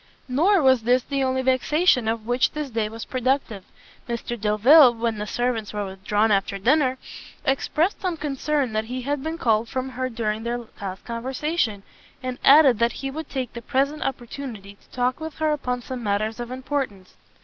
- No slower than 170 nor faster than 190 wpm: Yes, average, 180 wpm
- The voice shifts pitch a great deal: No, average, 3.6 semitones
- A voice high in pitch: Yes, very high, 250 Hz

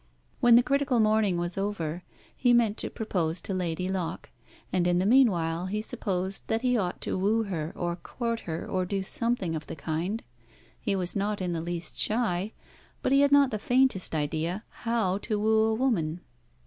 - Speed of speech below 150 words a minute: No, average, 190 wpm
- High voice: Yes, high, 195 Hz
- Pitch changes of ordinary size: Yes, average, 4.5 semitones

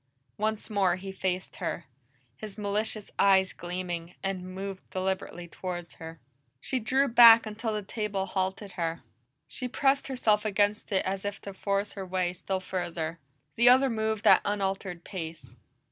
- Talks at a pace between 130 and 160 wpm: Yes, average, 155 wpm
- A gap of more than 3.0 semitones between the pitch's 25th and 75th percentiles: No, average, 2.7 semitones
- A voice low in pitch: No, high, 195 Hz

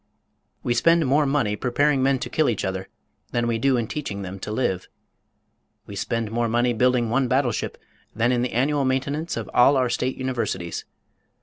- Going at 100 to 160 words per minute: No, average, 185 wpm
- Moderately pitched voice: No, low, 125 Hz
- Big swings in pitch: No, average, 3.0 semitones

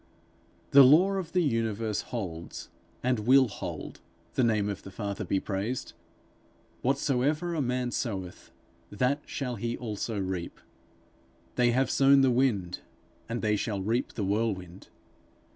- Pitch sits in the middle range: No, low, 115 Hz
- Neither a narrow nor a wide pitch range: Yes, average, 4.6 semitones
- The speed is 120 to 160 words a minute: Yes, average, 140 wpm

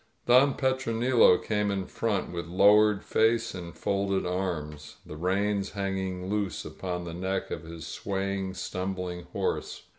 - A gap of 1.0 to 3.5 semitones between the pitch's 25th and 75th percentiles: Yes, average, 2.7 semitones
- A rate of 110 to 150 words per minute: Yes, average, 140 wpm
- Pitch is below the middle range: Yes, very low, 95 Hz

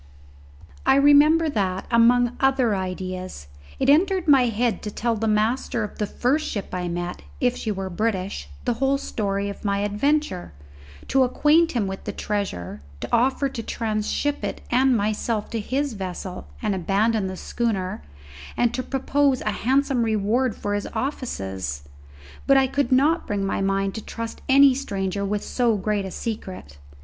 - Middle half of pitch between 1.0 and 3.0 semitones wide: No, average, 5.1 semitones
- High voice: Yes, high, 225 Hz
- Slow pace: No, average, 165 wpm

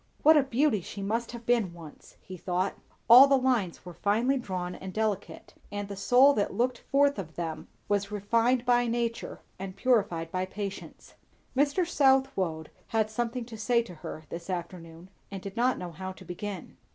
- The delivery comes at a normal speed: Yes, average, 180 wpm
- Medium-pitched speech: No, high, 210 Hz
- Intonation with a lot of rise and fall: No, average, 4.9 semitones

